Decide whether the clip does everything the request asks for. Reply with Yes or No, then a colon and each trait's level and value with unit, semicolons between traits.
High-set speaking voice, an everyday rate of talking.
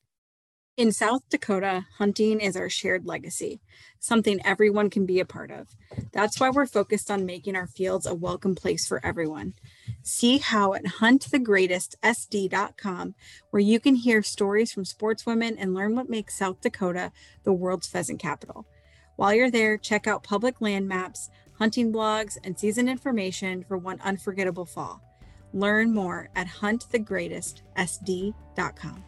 Yes: high, 200 Hz; average, 145 wpm